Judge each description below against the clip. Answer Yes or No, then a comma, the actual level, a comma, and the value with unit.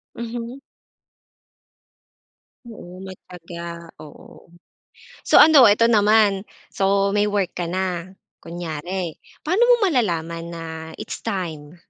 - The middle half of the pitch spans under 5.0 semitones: Yes, average, 4.6 semitones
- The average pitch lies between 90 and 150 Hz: No, high, 190 Hz